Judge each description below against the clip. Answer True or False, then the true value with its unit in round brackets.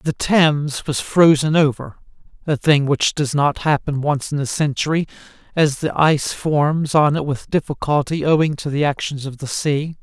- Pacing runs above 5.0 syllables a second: False (4.7 syllables/s)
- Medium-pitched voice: True (145 Hz)